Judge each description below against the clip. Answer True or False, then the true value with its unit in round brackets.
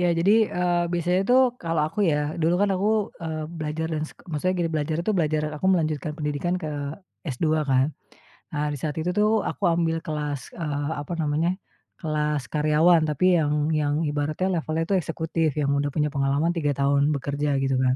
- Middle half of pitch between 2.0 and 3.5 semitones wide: True (2.5 semitones)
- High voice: False (155 Hz)